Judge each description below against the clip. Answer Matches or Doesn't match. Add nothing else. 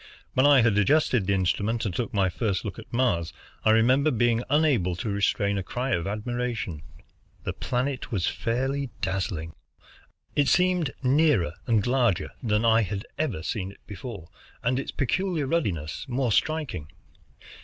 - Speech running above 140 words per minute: Matches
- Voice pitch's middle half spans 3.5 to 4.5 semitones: Doesn't match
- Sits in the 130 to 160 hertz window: Doesn't match